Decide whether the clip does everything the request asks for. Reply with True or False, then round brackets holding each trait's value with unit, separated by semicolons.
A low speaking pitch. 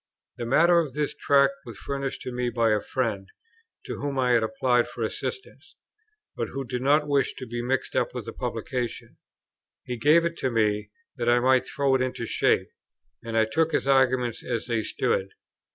True (125 Hz)